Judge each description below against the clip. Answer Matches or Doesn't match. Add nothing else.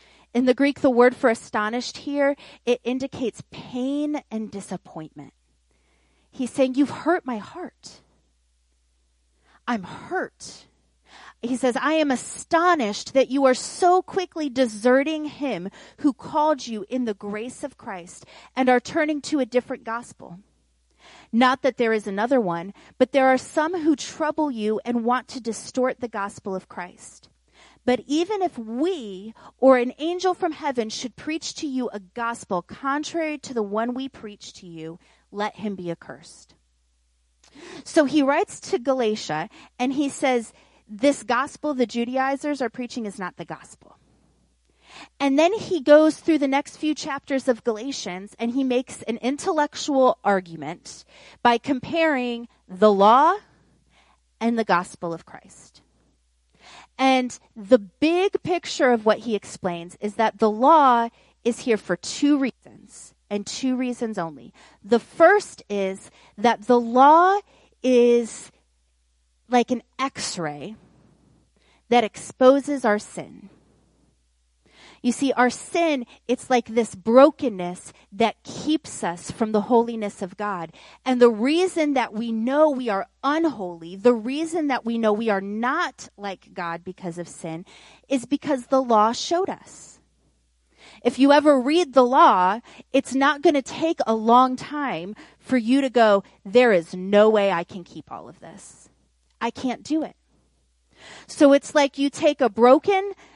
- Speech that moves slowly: Doesn't match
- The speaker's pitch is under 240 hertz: Doesn't match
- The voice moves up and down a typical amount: Doesn't match